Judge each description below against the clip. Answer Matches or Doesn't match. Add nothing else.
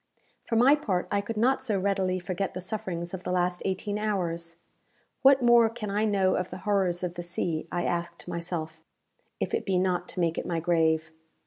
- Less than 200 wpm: Doesn't match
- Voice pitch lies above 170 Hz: Matches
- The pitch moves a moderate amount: Matches